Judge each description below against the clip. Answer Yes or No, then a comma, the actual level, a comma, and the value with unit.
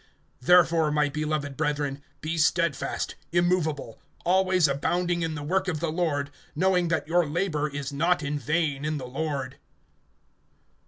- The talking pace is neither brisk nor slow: Yes, average, 145 wpm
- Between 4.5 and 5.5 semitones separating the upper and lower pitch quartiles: No, average, 3.2 semitones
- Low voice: No, medium, 155 Hz